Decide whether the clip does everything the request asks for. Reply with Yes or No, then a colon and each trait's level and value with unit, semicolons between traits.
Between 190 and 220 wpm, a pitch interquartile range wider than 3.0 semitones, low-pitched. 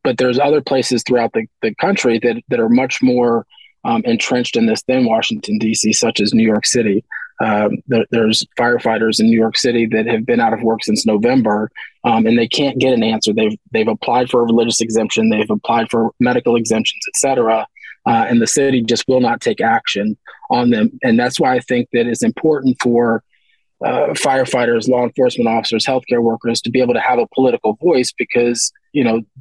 Yes: fast, 205 wpm; average, 3.5 semitones; low, 120 Hz